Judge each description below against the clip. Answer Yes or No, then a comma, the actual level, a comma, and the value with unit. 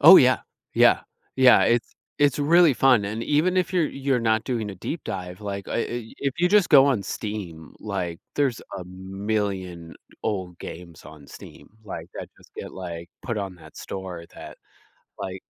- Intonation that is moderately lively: No, wide, 6.4 semitones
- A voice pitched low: Yes, low, 105 Hz